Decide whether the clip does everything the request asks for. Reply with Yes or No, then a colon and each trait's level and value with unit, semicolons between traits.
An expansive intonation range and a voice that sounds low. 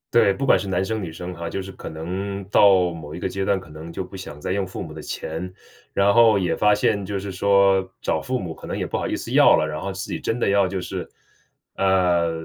No: narrow, 2.4 semitones; very low, 95 Hz